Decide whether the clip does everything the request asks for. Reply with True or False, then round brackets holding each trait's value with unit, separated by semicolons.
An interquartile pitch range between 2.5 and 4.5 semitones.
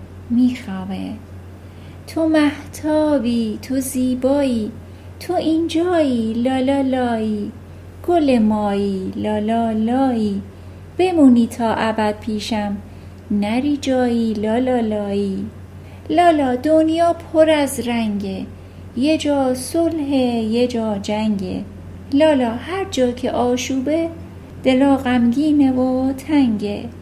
False (4.9 semitones)